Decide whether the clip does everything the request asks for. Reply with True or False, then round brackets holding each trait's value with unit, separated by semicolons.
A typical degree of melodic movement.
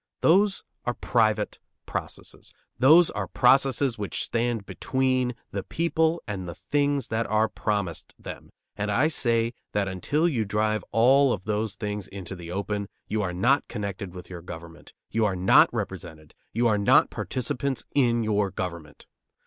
True (4.7 semitones)